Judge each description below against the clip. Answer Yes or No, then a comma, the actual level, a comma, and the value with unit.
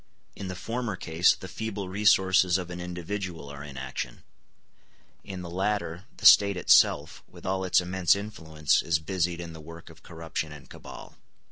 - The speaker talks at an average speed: Yes, average, 170 wpm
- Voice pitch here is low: Yes, very low, 90 Hz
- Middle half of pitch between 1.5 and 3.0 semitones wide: Yes, average, 2.7 semitones